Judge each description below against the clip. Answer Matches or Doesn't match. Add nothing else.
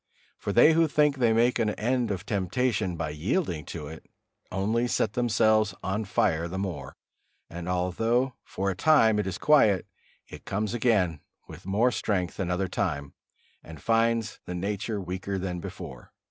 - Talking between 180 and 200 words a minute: Doesn't match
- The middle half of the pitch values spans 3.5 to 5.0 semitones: Matches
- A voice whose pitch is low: Matches